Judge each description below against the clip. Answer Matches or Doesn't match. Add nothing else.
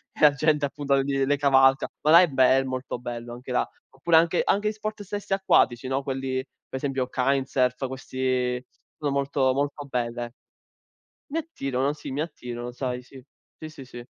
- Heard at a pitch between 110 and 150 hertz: Matches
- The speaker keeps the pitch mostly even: Matches